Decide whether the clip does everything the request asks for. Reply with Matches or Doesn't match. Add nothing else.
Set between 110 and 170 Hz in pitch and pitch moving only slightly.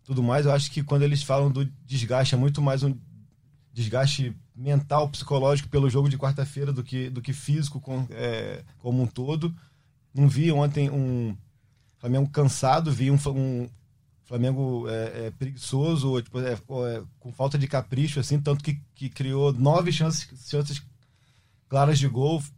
Matches